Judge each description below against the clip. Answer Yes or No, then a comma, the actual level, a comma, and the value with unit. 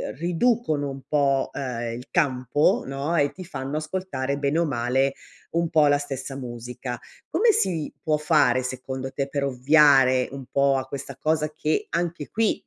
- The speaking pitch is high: No, medium, 140 Hz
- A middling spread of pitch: Yes, average, 3.0 semitones